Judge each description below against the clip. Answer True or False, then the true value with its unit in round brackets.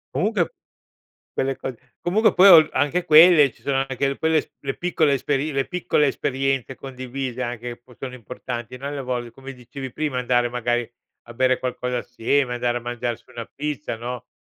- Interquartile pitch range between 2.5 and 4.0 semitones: True (2.8 semitones)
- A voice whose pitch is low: True (130 Hz)